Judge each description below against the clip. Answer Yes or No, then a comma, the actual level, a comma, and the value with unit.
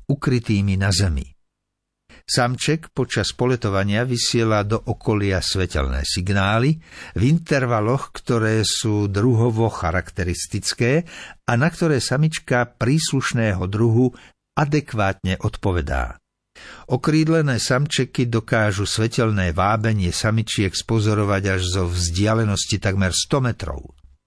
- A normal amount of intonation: Yes, average, 4.5 semitones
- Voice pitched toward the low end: Yes, low, 110 Hz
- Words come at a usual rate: No, slow, 95 wpm